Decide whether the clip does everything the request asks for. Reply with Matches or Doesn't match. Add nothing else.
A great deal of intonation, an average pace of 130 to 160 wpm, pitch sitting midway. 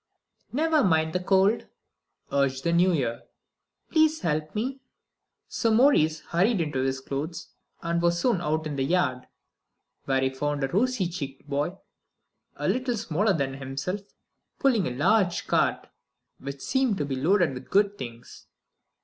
Matches